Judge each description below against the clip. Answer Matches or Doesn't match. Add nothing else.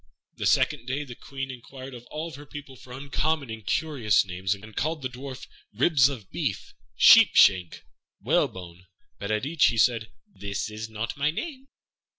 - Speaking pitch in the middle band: Doesn't match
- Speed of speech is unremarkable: Matches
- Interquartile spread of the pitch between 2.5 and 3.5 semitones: Doesn't match